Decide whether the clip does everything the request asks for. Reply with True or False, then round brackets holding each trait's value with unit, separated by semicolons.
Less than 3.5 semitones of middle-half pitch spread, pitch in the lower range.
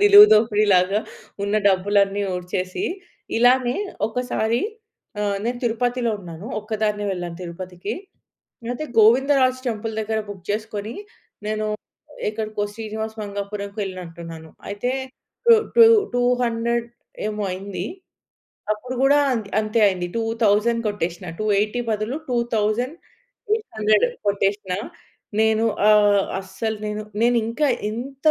False (2.8 semitones; 215 Hz)